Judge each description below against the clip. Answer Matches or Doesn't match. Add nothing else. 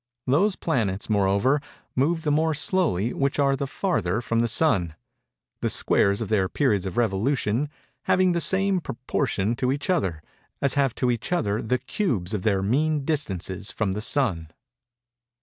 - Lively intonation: Matches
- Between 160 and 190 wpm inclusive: Matches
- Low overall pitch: Matches